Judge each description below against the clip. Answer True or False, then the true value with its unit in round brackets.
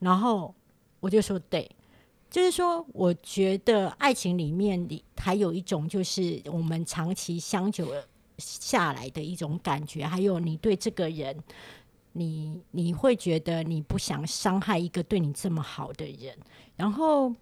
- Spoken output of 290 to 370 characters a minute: False (225 characters per minute)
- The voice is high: False (180 Hz)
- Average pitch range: True (3.9 semitones)